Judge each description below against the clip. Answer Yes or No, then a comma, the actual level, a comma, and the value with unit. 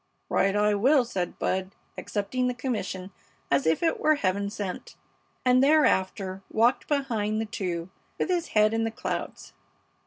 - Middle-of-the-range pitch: No, high, 215 Hz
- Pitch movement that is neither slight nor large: Yes, average, 5.0 semitones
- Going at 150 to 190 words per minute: Yes, average, 155 wpm